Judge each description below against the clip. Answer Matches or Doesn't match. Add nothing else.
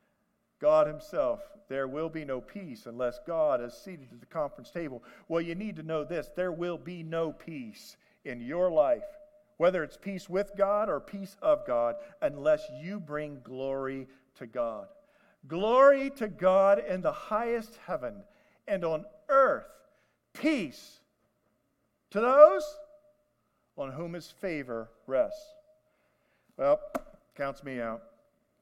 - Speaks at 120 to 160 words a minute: Matches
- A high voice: Matches